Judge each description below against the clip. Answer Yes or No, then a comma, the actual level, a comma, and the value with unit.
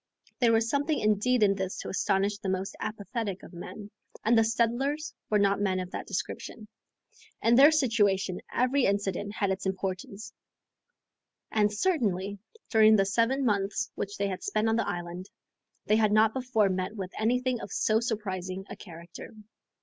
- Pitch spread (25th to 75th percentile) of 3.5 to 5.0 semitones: No, average, 3.0 semitones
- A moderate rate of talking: Yes, average, 165 wpm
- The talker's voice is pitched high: Yes, high, 210 Hz